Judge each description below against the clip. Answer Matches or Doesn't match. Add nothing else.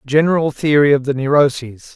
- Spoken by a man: Matches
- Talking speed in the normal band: Matches